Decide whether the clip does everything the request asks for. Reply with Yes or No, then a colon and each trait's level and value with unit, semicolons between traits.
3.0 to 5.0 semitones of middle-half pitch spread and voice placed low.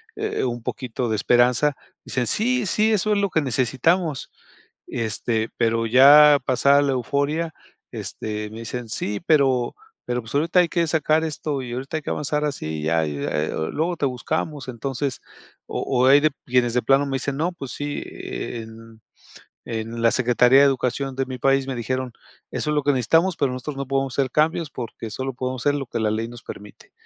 Yes: average, 3.8 semitones; low, 130 Hz